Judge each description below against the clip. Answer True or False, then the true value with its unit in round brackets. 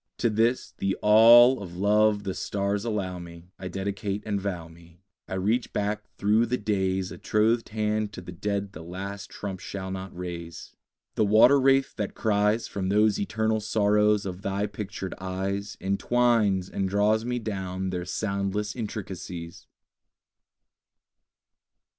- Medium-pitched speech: False (100 Hz)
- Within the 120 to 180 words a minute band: True (145 wpm)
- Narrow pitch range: True (2.3 semitones)